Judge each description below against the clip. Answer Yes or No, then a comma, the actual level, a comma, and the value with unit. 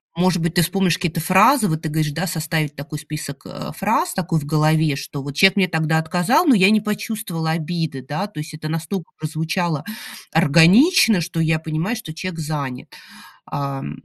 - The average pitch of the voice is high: No, medium, 160 Hz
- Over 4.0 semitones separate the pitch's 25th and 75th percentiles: No, average, 3.2 semitones